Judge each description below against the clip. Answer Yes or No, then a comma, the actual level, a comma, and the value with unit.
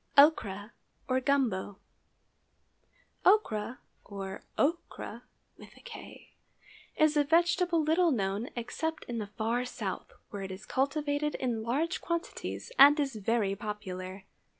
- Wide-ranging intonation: Yes, wide, 6.8 semitones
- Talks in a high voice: Yes, very high, 250 Hz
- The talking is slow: Yes, slow, 110 wpm